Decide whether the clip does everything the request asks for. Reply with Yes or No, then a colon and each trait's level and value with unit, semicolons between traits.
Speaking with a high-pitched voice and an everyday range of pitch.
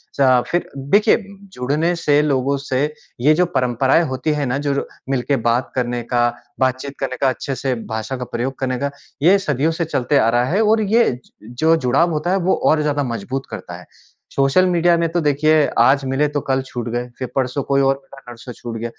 No: low, 135 Hz; average, 3.4 semitones